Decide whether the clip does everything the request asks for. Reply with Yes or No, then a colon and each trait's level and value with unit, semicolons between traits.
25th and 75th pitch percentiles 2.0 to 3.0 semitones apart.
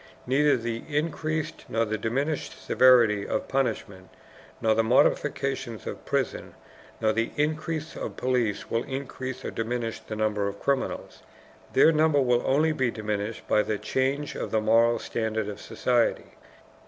No: average, 4.2 semitones